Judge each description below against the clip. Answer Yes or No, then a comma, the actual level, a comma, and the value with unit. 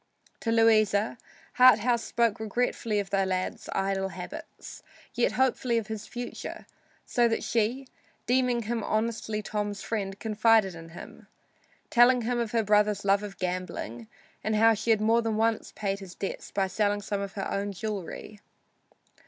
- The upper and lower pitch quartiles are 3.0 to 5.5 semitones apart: No, narrow, 2.6 semitones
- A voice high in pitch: Yes, high, 215 Hz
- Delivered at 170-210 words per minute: No, average, 160 wpm